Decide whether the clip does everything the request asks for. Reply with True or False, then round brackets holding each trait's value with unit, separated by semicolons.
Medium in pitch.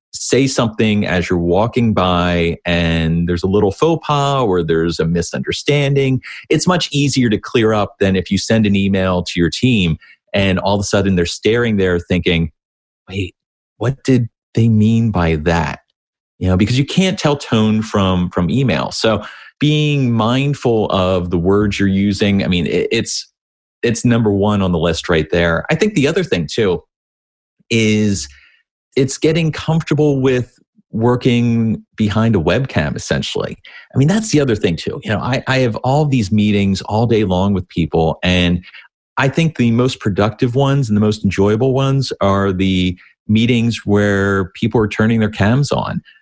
False (105 Hz)